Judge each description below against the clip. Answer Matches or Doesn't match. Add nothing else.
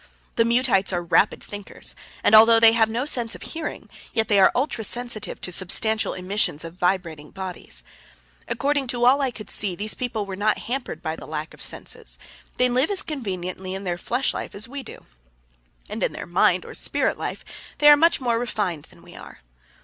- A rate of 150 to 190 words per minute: Doesn't match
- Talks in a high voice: Matches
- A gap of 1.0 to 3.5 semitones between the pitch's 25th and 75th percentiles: Doesn't match